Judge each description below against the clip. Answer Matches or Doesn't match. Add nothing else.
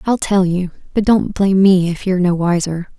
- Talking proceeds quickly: Matches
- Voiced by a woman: Matches